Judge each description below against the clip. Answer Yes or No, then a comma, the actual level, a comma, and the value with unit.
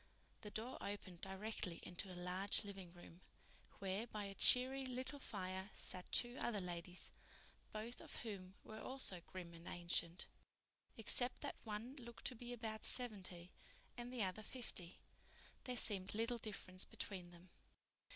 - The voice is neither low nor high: No, high, 205 Hz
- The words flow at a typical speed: Yes, average, 150 wpm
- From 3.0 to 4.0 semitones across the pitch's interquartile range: No, average, 4.5 semitones